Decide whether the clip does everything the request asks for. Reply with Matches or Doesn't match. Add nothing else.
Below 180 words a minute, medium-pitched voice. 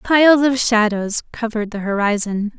Doesn't match